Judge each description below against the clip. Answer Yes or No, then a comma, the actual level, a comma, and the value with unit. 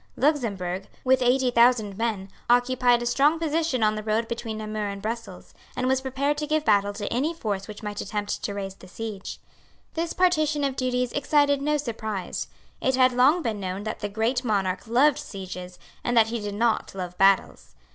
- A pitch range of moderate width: Yes, average, 4.4 semitones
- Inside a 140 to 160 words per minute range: No, average, 190 wpm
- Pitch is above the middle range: Yes, high, 230 Hz